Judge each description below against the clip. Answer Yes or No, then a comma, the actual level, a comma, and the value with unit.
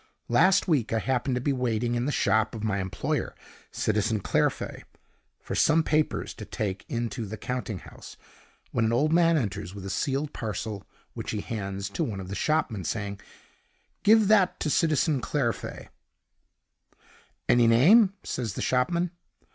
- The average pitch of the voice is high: No, low, 120 Hz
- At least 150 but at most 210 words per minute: Yes, average, 160 wpm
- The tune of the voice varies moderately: No, wide, 6.3 semitones